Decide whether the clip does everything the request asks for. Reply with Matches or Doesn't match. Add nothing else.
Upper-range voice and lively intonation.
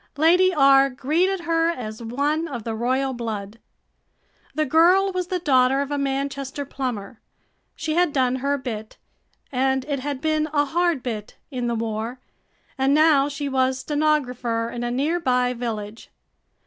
Doesn't match